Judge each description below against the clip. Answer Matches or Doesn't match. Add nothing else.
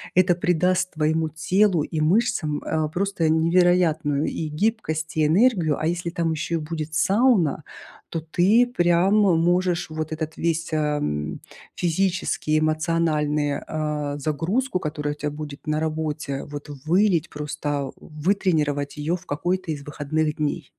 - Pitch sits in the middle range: Matches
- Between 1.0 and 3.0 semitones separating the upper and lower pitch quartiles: Matches